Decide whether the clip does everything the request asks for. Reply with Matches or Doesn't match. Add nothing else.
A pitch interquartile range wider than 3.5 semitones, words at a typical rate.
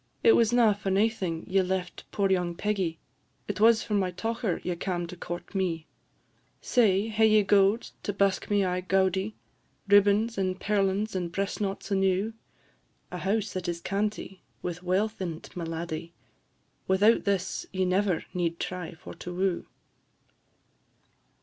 Doesn't match